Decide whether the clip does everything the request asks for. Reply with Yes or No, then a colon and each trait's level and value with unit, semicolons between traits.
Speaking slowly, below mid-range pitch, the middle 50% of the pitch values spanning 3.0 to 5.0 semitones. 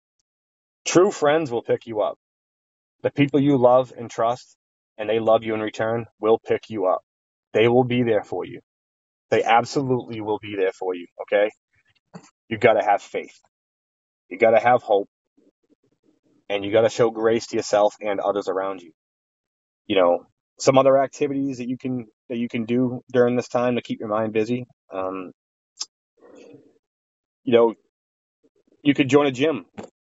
No: average, 170 wpm; low, 115 Hz; average, 4.0 semitones